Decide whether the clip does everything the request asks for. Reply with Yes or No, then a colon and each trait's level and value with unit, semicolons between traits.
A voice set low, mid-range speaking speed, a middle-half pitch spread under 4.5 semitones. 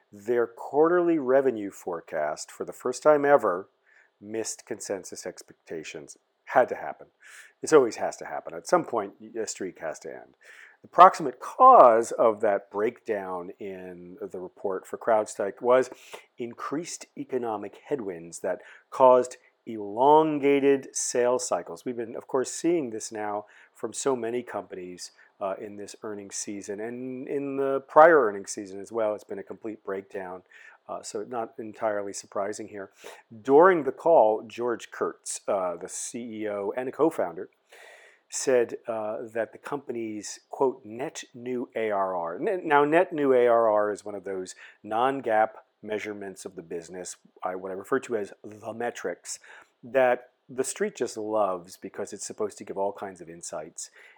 Yes: low, 110 Hz; average, 155 wpm; average, 4.1 semitones